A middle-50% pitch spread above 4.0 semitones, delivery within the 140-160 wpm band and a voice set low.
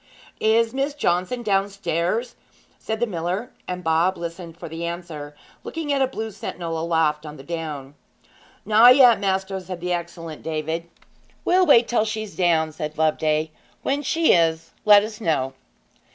No: average, 5.3 semitones; average, 155 wpm; medium, 180 Hz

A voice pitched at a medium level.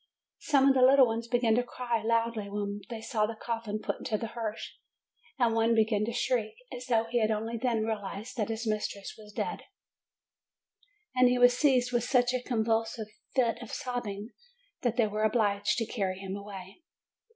No: high, 225 Hz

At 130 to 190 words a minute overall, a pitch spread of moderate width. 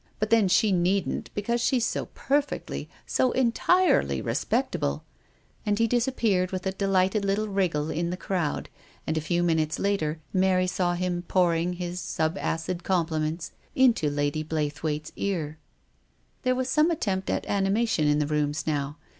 Yes: average, 165 wpm; average, 4.6 semitones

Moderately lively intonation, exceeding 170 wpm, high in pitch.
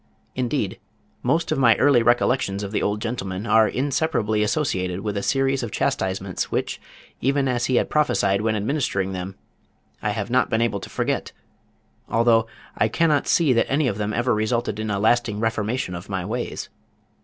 No: average, 3.9 semitones; average, 180 wpm; low, 115 Hz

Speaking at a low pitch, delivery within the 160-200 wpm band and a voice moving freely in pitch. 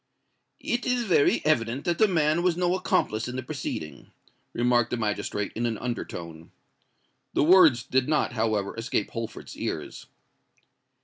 No: low, 125 Hz; average, 150 wpm; wide, 6.6 semitones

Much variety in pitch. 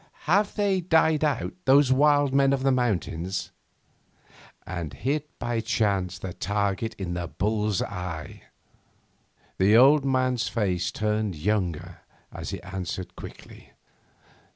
Yes: wide, 6.6 semitones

